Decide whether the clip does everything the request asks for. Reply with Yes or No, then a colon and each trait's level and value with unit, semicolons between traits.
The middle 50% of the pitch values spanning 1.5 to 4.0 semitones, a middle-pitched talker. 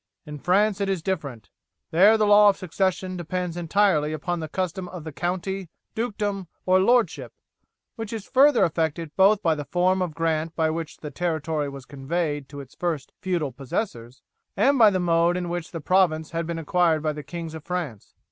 Yes: average, 3.4 semitones; medium, 175 Hz